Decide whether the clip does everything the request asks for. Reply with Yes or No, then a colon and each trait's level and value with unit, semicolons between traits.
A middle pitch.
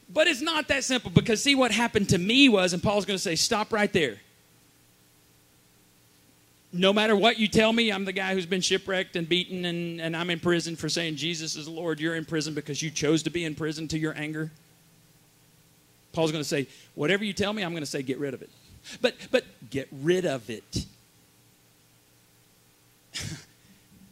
Yes: medium, 165 Hz